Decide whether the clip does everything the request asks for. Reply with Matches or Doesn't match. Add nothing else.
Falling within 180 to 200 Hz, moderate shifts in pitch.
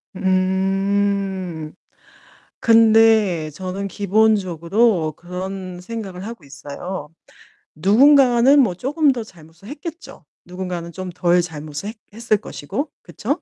Matches